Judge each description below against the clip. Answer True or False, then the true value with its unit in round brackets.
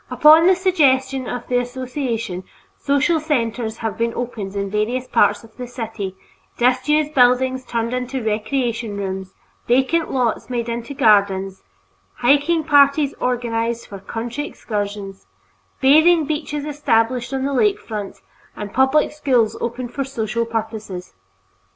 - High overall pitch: True (245 Hz)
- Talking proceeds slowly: True (130 wpm)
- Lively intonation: False (3.9 semitones)